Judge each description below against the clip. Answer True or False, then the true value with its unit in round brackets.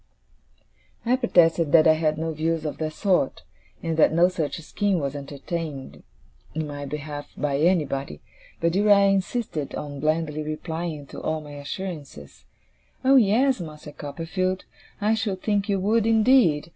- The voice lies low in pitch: False (165 Hz)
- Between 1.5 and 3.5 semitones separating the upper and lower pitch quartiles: False (4.6 semitones)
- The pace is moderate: True (150 wpm)